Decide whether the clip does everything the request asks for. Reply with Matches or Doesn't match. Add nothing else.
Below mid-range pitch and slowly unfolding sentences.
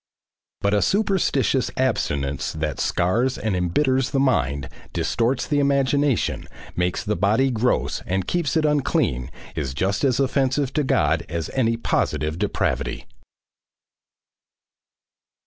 Matches